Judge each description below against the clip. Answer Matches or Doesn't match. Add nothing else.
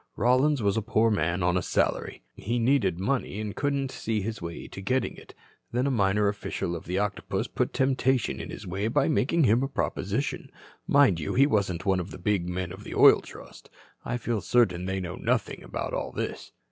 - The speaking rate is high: Matches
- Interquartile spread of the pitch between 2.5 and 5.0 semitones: Doesn't match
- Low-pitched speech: Matches